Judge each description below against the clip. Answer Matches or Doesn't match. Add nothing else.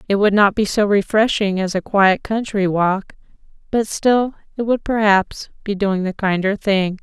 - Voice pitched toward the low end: Doesn't match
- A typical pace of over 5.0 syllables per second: Doesn't match